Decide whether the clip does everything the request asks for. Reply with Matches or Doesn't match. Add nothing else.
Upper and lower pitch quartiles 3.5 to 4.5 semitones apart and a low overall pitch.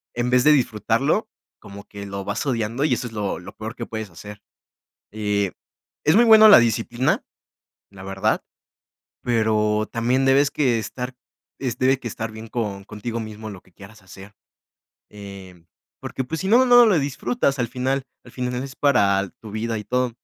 Matches